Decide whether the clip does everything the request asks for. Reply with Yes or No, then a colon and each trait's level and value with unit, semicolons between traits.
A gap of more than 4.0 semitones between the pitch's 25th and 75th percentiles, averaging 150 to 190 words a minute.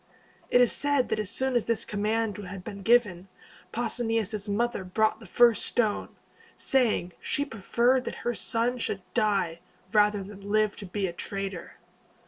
No: average, 3.2 semitones; average, 160 wpm